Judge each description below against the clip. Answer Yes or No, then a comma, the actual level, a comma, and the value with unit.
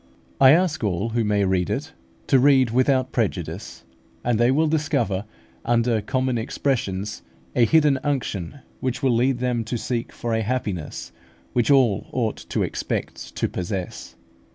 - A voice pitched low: Yes, low, 120 Hz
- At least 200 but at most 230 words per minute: No, average, 155 wpm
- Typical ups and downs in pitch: Yes, average, 4.1 semitones